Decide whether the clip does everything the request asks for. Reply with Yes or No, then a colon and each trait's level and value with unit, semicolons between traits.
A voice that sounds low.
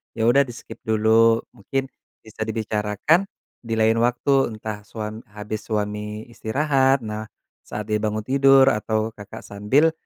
Yes: low, 110 Hz